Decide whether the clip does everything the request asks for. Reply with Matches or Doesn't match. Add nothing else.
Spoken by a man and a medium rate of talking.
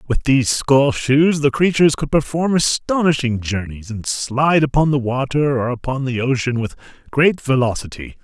Matches